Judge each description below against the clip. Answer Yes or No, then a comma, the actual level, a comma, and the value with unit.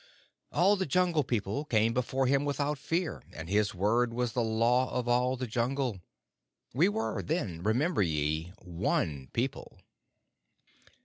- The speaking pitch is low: Yes, low, 125 Hz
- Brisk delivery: No, average, 140 wpm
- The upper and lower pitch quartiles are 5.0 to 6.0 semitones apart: Yes, average, 5.3 semitones